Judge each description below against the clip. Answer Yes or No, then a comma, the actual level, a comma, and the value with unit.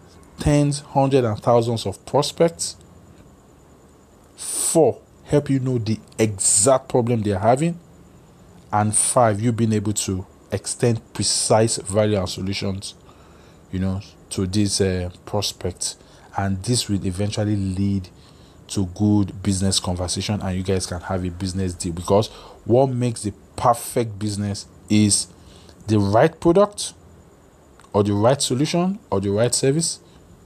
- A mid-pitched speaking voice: No, low, 100 Hz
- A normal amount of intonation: Yes, average, 4.2 semitones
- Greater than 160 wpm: No, slow, 135 wpm